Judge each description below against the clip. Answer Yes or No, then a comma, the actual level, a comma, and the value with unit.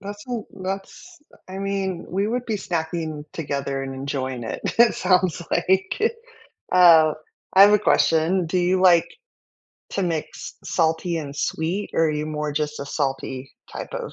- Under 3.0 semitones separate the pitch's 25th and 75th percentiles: No, average, 4.2 semitones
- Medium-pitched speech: Yes, medium, 170 Hz